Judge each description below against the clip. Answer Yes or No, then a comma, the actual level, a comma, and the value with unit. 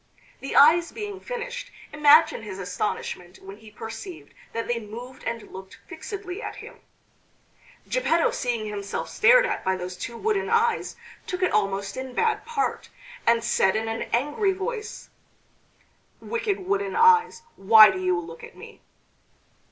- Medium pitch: No, very high, 265 Hz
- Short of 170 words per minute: Yes, average, 150 wpm